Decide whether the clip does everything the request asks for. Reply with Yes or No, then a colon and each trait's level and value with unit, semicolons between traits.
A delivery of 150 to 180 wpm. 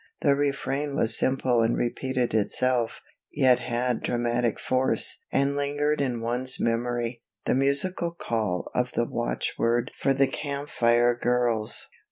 No: slow, 135 wpm